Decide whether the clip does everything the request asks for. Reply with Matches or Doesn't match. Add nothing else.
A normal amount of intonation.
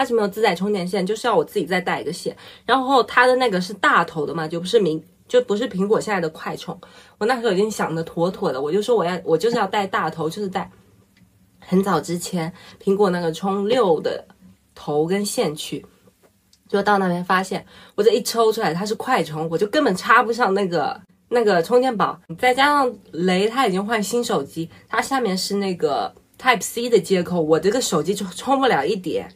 Doesn't match